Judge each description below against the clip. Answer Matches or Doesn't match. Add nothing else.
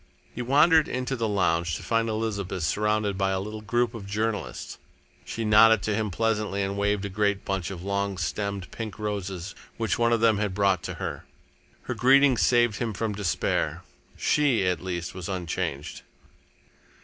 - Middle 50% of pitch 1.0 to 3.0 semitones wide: Matches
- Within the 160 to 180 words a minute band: Matches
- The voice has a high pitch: Doesn't match